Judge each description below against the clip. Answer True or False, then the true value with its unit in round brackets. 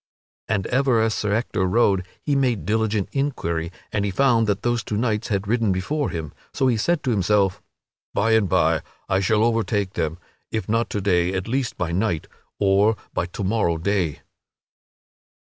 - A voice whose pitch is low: True (105 Hz)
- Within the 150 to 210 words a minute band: True (180 wpm)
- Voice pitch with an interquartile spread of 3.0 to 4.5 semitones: True (3.5 semitones)